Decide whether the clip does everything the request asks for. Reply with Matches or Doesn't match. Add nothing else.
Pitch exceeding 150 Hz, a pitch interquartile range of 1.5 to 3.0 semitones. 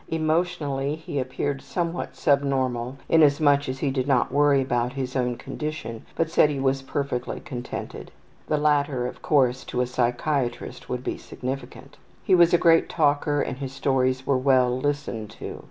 Doesn't match